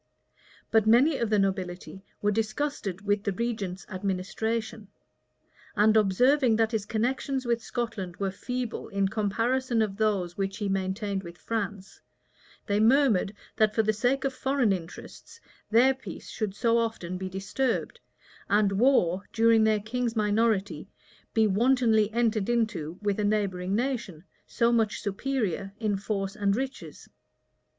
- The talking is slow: No, average, 145 wpm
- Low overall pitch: No, high, 215 Hz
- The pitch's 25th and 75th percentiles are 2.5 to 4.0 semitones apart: Yes, average, 3.1 semitones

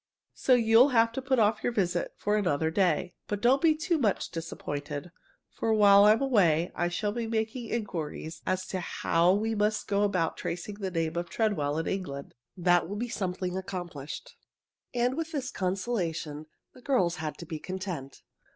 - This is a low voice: No, high, 195 Hz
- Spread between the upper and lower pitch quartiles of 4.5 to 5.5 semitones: Yes, average, 4.9 semitones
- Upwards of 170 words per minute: Yes, average, 180 wpm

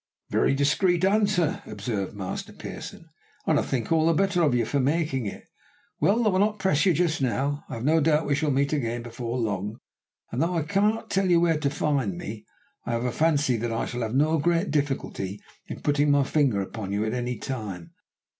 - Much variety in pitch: Yes, wide, 5.9 semitones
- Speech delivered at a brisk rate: Yes, fast, 215 wpm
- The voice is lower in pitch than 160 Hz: Yes, medium, 140 Hz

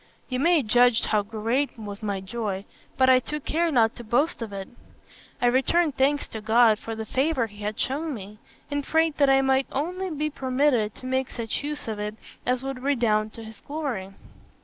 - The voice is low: No, very high, 250 Hz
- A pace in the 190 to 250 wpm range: Yes, average, 200 wpm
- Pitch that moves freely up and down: No, average, 4.7 semitones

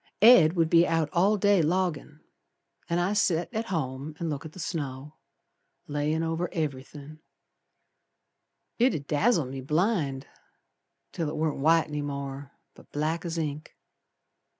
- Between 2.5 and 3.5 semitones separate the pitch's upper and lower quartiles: Yes, average, 3.1 semitones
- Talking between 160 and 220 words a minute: No, average, 145 wpm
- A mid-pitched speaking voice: Yes, medium, 160 Hz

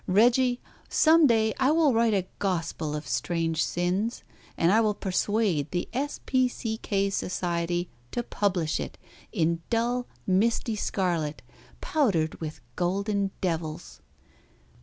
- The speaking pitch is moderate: No, high, 195 Hz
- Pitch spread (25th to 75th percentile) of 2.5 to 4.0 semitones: No, wide, 5.4 semitones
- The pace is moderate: No, slow, 130 wpm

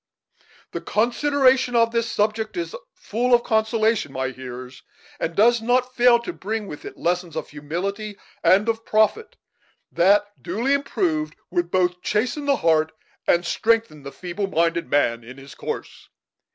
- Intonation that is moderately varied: No, wide, 5.8 semitones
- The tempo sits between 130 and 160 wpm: Yes, average, 150 wpm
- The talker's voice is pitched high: Yes, high, 205 Hz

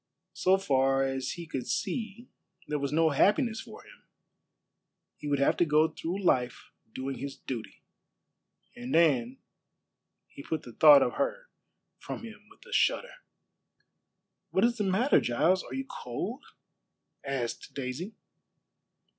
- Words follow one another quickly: No, average, 140 wpm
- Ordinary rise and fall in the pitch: No, wide, 7.9 semitones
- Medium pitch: Yes, medium, 160 Hz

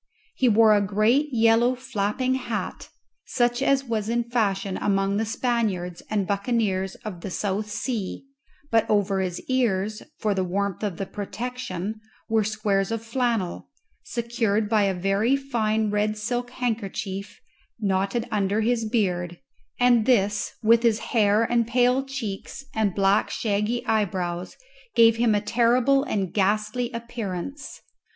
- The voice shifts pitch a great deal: No, average, 3.2 semitones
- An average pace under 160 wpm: Yes, average, 140 wpm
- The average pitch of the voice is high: Yes, high, 215 Hz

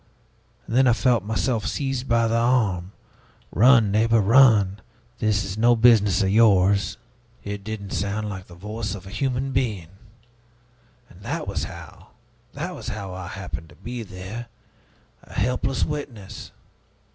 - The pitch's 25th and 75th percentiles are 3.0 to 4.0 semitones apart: Yes, average, 3.5 semitones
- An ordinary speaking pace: Yes, average, 150 wpm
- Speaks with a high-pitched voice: No, low, 110 Hz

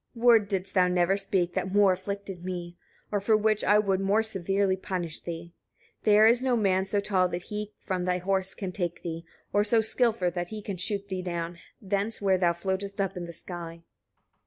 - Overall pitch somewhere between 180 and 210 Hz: Yes, high, 190 Hz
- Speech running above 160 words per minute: Yes, fast, 205 wpm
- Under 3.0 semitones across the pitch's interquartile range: Yes, narrow, 2.5 semitones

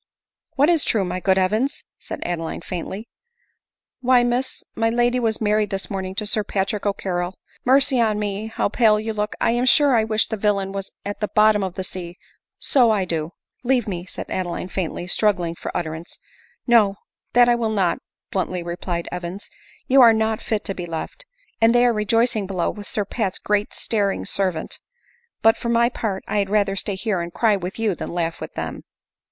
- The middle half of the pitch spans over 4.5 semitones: No, average, 3.4 semitones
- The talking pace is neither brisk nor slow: No, fast, 215 wpm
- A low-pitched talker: No, high, 210 Hz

